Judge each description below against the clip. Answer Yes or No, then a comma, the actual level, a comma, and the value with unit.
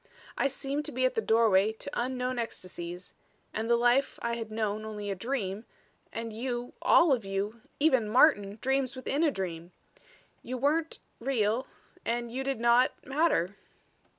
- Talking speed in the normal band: Yes, average, 160 wpm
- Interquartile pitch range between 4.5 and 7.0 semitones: No, average, 3.9 semitones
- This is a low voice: No, high, 235 Hz